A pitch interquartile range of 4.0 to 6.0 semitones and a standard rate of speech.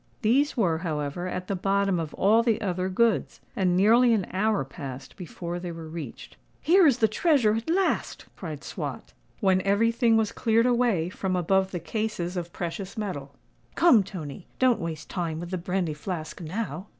Yes: average, 4.6 semitones; average, 175 wpm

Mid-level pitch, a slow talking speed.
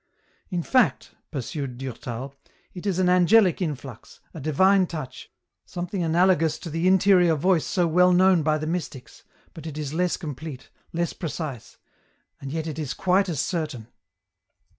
No: medium, 165 Hz; average, 160 wpm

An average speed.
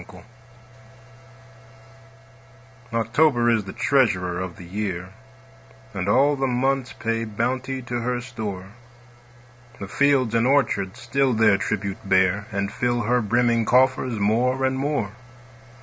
No: slow, 125 wpm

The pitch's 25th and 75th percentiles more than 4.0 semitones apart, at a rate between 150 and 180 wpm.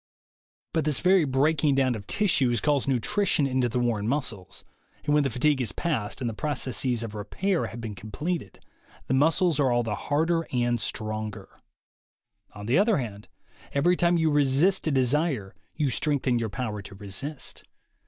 Yes: average, 5.2 semitones; average, 170 wpm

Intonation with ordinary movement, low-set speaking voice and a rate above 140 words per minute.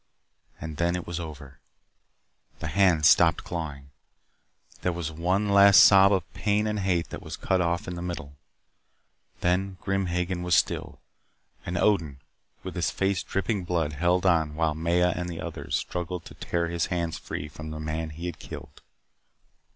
No: narrow, 2.3 semitones; very low, 85 Hz; average, 170 wpm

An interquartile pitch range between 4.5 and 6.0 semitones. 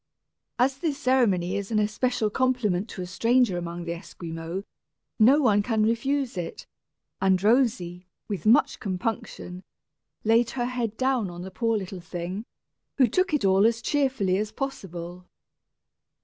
Yes: average, 5.3 semitones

